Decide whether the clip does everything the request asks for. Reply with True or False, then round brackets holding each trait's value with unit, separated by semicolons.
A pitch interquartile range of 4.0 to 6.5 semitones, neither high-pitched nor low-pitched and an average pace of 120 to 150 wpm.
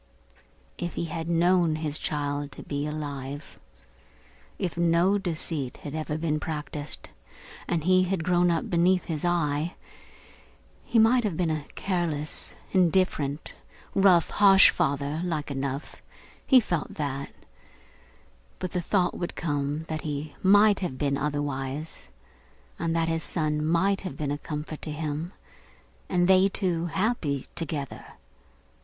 False (3.3 semitones; 160 Hz; 135 wpm)